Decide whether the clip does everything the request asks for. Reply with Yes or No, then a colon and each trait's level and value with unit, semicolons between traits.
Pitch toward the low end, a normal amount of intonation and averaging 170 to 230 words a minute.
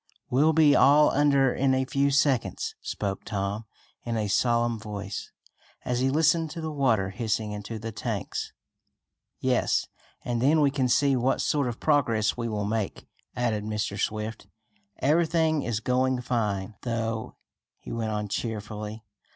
No: low, 120 Hz; average, 4.5 semitones; average, 150 wpm